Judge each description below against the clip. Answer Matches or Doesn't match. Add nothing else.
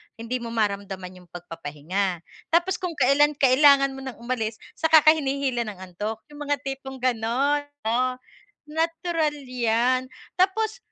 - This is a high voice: Matches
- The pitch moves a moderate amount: Matches